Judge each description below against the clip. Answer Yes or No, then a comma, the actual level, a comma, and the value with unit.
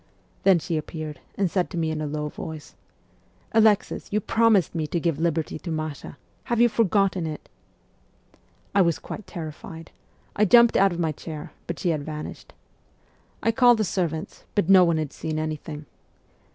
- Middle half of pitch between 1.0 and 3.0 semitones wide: No, average, 4.1 semitones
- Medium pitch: Yes, medium, 170 Hz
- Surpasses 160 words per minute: Yes, average, 180 wpm